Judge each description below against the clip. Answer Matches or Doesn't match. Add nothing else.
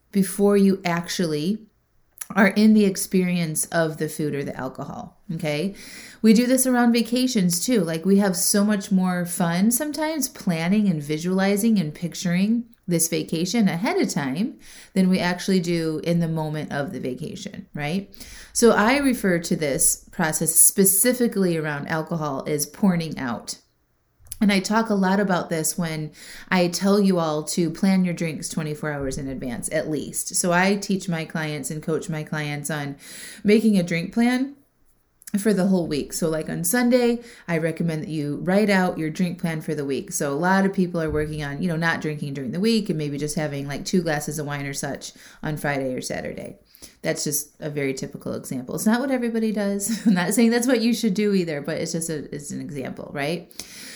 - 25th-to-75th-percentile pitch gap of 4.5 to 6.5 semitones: Matches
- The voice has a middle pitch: Matches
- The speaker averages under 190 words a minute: Doesn't match